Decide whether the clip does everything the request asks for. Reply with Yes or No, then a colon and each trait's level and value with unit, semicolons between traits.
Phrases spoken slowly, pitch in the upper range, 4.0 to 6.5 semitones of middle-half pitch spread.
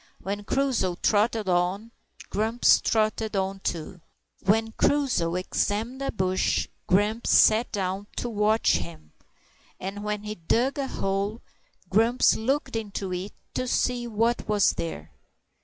No: slow, 130 wpm; high, 210 Hz; average, 3.3 semitones